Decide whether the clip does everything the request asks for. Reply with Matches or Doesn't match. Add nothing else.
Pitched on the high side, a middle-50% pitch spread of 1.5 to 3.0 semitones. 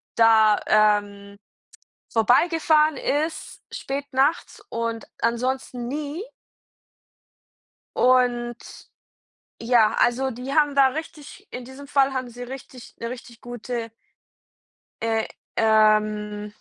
Doesn't match